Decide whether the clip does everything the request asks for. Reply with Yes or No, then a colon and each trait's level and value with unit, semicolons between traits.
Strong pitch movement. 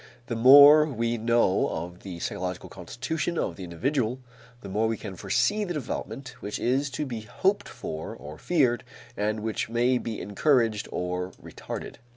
Yes: wide, 5.8 semitones